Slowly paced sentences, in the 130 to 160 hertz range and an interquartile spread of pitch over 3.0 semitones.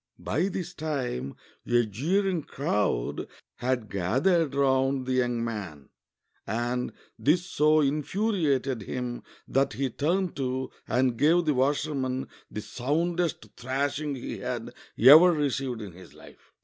Yes: slow, 125 wpm; low, 135 Hz; average, 4.1 semitones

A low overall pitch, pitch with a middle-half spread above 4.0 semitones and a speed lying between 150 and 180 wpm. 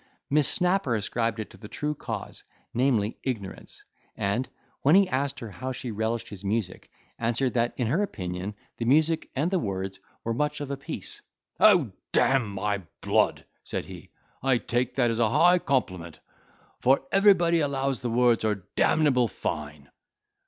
Yes: low, 125 Hz; average, 5.2 semitones; average, 165 wpm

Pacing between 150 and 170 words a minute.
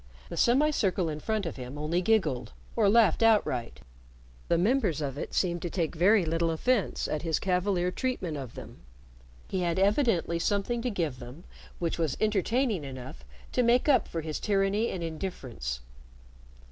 Yes: average, 165 wpm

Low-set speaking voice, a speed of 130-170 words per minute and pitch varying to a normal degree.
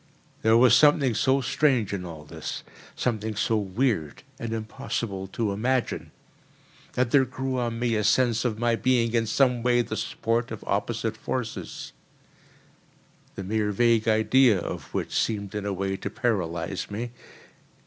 Yes: low, 115 Hz; average, 150 wpm; average, 3.0 semitones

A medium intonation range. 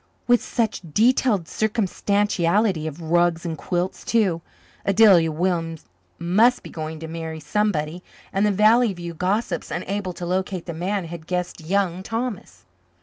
Yes: average, 3.9 semitones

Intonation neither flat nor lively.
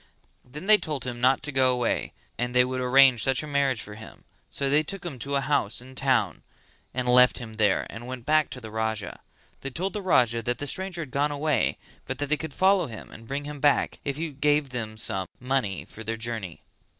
Yes: average, 3.8 semitones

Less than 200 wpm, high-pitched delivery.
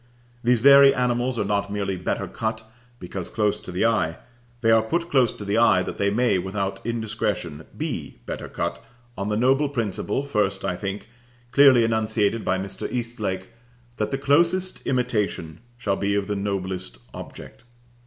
No: average, 165 wpm; low, 110 Hz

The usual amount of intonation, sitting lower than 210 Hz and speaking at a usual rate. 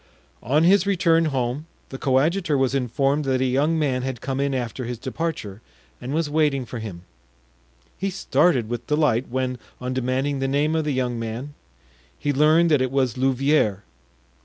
Yes: average, 3.3 semitones; low, 135 Hz; average, 175 wpm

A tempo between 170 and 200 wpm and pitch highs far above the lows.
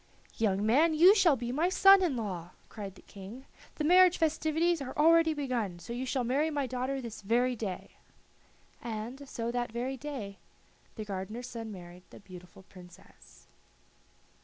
No: average, 160 wpm; wide, 6.1 semitones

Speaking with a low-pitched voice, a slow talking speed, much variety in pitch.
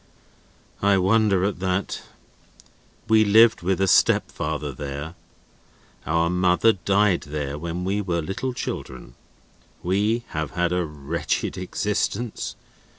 No: very low, 90 Hz; slow, 115 wpm; average, 3.5 semitones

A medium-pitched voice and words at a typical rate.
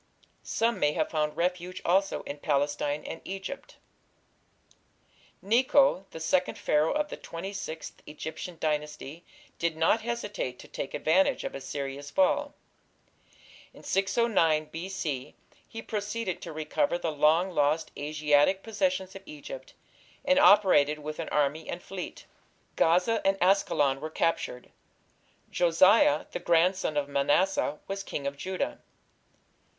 No: medium, 170 Hz; slow, 130 wpm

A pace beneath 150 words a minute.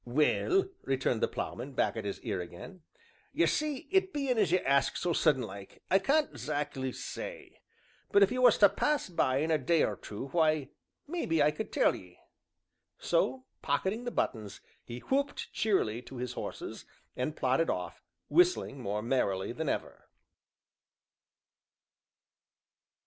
No: average, 155 wpm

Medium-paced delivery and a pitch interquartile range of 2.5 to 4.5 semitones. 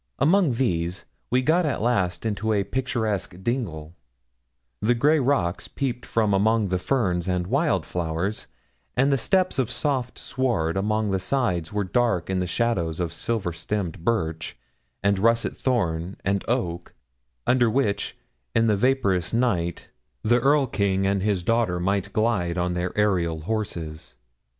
No: average, 150 wpm; wide, 5.5 semitones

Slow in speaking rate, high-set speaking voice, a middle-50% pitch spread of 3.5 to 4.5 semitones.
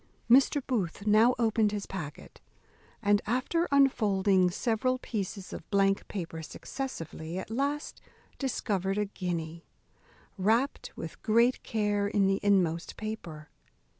Yes: slow, 120 wpm; high, 205 Hz; average, 4.0 semitones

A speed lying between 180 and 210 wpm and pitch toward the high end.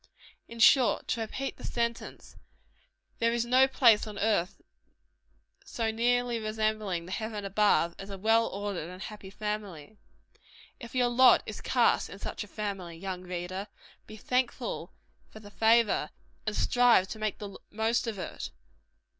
No: average, 155 wpm; high, 215 Hz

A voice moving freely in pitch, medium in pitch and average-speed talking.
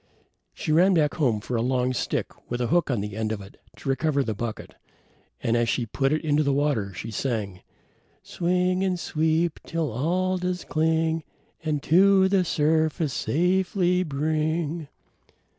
Yes: wide, 5.7 semitones; medium, 155 Hz; average, 165 wpm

